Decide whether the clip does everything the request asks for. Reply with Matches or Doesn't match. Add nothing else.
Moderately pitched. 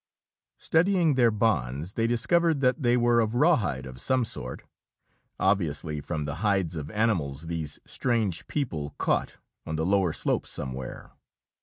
Doesn't match